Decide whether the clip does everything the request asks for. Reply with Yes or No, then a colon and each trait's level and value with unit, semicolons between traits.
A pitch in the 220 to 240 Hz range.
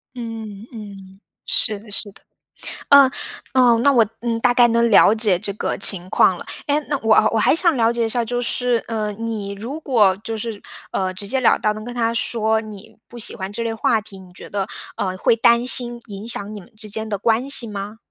Yes: high, 225 Hz